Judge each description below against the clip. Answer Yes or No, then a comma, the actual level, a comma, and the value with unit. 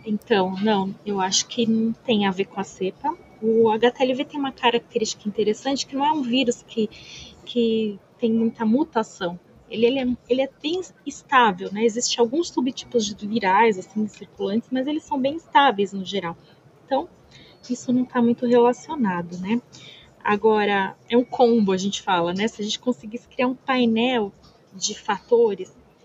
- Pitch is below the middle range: No, high, 230 Hz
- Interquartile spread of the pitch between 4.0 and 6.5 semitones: No, average, 3.5 semitones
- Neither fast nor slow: Yes, average, 170 wpm